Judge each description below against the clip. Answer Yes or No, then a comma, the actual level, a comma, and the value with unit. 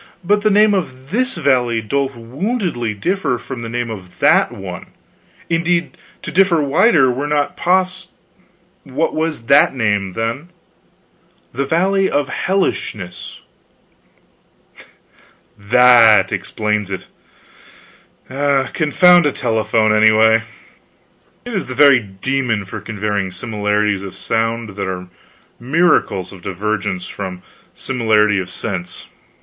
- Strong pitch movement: Yes, wide, 7.5 semitones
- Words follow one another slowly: Yes, slow, 120 wpm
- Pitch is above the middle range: No, low, 120 Hz